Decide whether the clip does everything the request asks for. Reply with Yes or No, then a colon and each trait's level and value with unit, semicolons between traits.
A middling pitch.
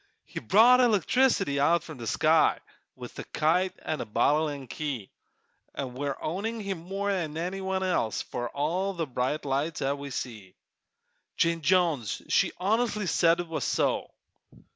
Yes: medium, 165 Hz